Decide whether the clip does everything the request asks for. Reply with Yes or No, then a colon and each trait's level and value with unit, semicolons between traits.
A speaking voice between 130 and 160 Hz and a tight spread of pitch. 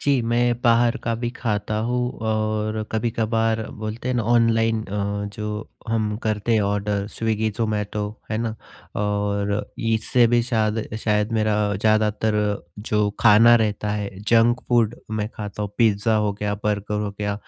No: low, 110 Hz; narrow, 1.6 semitones